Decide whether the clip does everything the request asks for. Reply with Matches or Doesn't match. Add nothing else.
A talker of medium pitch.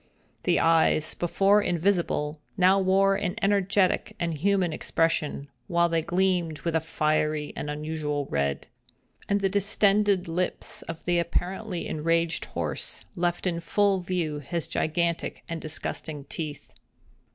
Matches